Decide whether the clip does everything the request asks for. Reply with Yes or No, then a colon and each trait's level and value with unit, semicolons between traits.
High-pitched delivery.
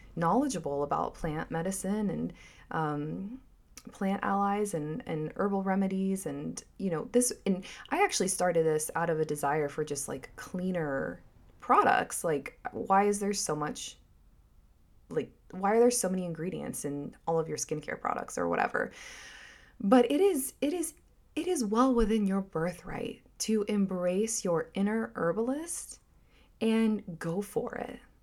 Yes: high, 195 Hz